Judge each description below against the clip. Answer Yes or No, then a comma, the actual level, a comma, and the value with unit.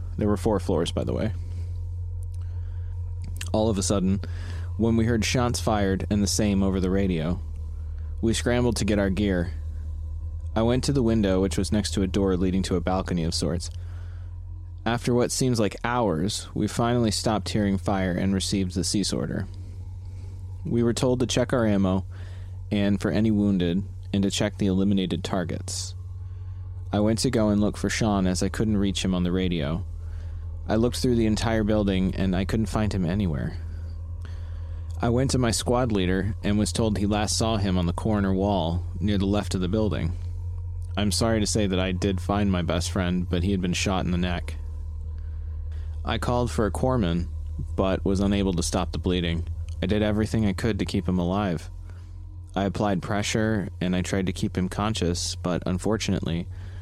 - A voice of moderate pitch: No, very low, 95 Hz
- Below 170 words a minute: No, average, 190 wpm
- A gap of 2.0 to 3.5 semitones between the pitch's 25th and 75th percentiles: Yes, average, 2.9 semitones